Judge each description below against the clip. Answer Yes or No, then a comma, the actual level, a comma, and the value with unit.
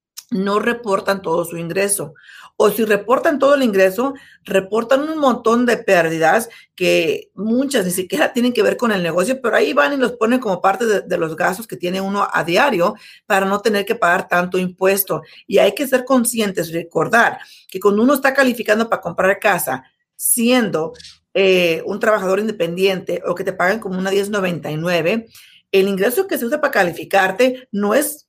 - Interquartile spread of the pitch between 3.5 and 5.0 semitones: Yes, average, 4.6 semitones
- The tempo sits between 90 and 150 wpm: No, average, 180 wpm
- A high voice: Yes, high, 205 Hz